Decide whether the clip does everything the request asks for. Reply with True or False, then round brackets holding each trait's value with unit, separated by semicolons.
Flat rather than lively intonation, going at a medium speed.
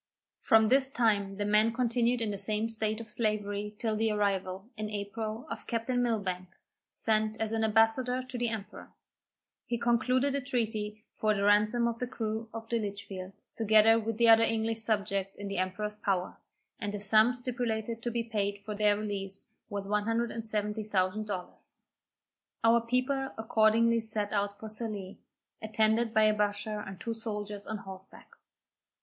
True (1.9 semitones; 165 wpm)